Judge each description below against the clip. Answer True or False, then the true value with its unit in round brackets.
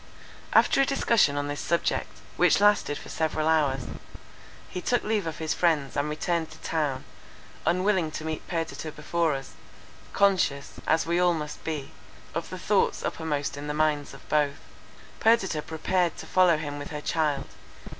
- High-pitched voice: False (160 Hz)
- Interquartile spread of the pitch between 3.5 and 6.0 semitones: False (2.9 semitones)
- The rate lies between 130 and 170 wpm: True (165 wpm)